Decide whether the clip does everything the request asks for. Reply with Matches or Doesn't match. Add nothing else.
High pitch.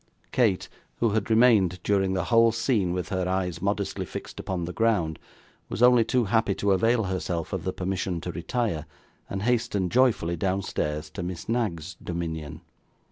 Doesn't match